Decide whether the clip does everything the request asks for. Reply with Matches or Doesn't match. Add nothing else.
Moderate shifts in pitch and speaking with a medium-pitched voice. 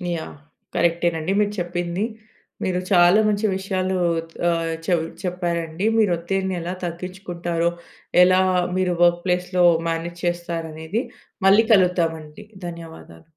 Doesn't match